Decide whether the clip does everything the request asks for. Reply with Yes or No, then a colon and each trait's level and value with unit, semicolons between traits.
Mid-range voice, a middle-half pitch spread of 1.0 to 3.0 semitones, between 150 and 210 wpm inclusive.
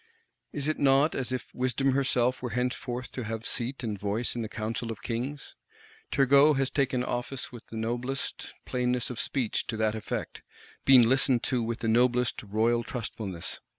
No: low, 125 Hz; narrow, 2.6 semitones; average, 175 wpm